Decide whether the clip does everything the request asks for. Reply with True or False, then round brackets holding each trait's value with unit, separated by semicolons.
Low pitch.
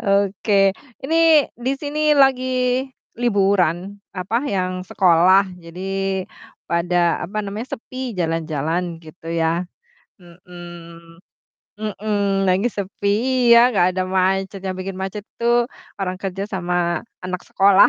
False (195 Hz)